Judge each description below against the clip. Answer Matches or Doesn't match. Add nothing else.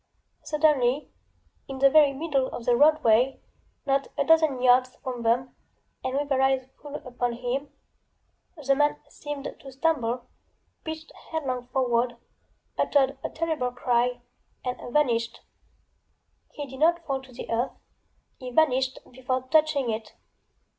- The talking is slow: Matches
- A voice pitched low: Doesn't match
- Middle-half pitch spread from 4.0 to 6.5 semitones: Doesn't match